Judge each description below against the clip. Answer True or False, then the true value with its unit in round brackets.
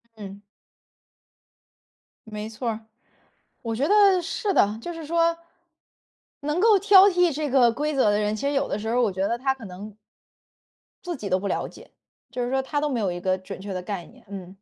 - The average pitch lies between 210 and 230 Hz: False (240 Hz)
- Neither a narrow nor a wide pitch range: False (6.8 semitones)